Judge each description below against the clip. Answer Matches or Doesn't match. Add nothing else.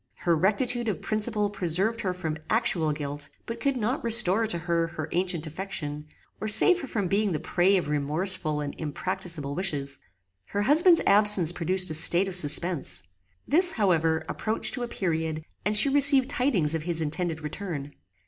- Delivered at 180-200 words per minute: Doesn't match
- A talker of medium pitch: Matches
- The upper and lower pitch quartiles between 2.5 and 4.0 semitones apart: Doesn't match